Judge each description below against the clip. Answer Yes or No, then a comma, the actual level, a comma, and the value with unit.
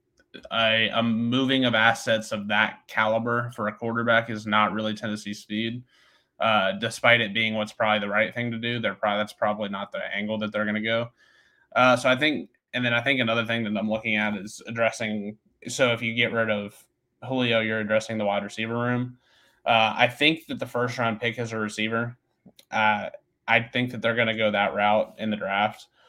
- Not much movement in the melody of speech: Yes, narrow, 1.8 semitones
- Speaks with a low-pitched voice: Yes, low, 115 Hz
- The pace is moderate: No, fast, 210 wpm